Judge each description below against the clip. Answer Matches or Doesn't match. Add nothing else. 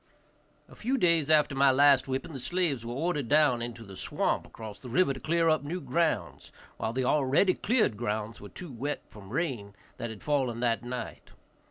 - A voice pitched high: Doesn't match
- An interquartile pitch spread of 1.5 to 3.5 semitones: Doesn't match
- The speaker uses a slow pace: Doesn't match